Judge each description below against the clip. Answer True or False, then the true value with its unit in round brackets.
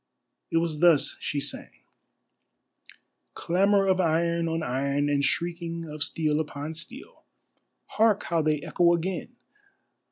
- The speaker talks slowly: True (125 wpm)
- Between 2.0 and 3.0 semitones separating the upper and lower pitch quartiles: True (2.4 semitones)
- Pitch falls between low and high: True (165 Hz)